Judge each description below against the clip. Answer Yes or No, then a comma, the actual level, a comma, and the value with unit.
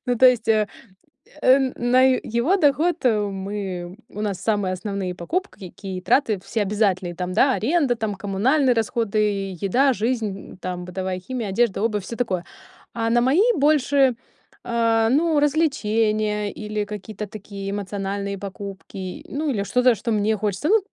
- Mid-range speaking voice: No, high, 215 Hz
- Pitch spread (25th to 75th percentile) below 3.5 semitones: No, average, 4.2 semitones